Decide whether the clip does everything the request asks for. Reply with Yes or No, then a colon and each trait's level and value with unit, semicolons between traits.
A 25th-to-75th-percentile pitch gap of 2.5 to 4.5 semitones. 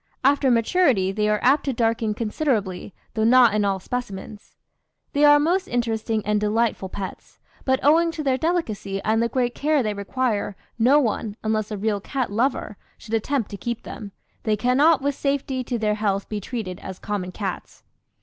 Yes: average, 4.2 semitones